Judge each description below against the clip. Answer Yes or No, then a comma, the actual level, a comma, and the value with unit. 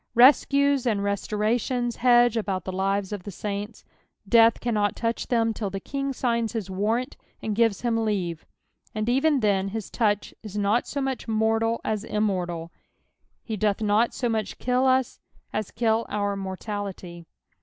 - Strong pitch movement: No, average, 2.8 semitones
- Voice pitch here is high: Yes, high, 220 Hz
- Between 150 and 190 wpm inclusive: Yes, average, 160 wpm